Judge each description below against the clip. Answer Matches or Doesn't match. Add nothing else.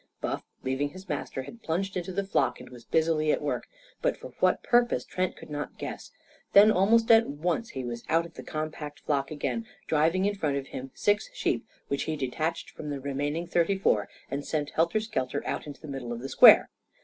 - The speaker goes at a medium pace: Doesn't match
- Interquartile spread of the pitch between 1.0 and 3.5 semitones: Doesn't match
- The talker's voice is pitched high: Doesn't match